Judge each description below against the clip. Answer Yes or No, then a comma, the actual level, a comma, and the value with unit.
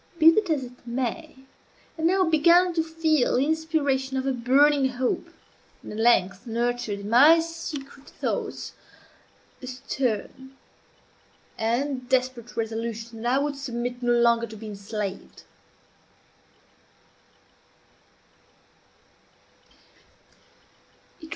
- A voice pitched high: Yes, very high, 255 Hz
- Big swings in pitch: No, average, 3.9 semitones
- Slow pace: Yes, slow, 105 wpm